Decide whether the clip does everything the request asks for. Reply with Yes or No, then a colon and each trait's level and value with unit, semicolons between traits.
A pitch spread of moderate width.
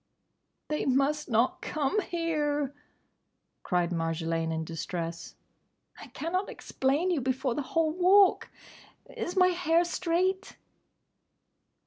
No: wide, 8.1 semitones